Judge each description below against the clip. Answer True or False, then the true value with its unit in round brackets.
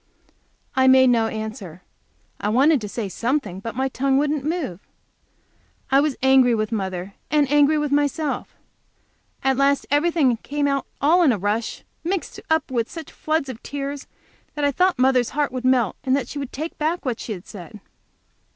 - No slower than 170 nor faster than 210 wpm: True (180 wpm)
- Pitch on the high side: True (265 Hz)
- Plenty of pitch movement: False (4.2 semitones)